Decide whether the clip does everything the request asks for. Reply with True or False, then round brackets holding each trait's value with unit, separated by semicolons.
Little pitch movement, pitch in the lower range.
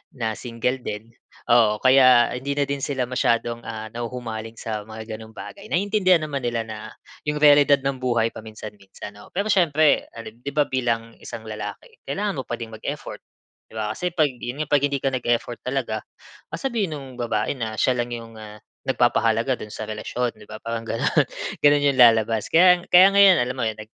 False (4.1 semitones; 120 Hz)